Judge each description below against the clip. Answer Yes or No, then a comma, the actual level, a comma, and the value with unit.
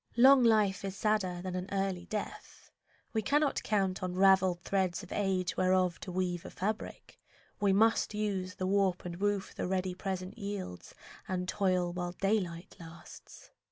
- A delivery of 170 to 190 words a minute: No, average, 160 wpm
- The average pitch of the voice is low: No, high, 190 Hz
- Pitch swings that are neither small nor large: No, narrow, 1.9 semitones